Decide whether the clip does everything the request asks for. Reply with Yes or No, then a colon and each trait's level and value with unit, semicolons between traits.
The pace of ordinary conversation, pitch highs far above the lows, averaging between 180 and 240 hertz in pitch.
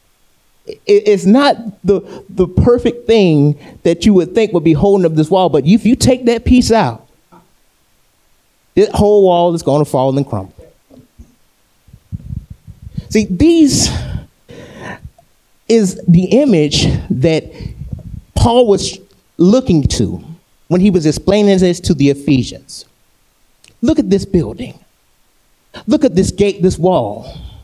No: slow, 130 wpm; wide, 5.8 semitones; medium, 185 Hz